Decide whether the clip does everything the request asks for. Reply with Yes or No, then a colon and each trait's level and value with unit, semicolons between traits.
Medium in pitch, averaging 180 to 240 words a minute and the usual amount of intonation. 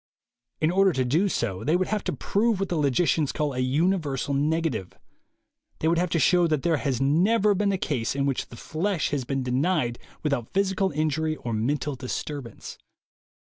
Yes: medium, 155 Hz; average, 185 wpm; average, 5.0 semitones